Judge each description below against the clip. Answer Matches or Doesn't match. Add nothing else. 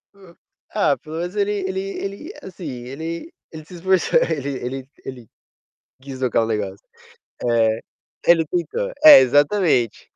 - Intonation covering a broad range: Matches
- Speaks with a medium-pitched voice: Matches